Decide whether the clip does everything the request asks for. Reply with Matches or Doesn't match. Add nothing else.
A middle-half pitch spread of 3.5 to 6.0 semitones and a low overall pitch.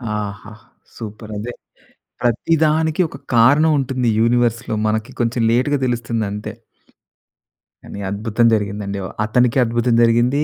Doesn't match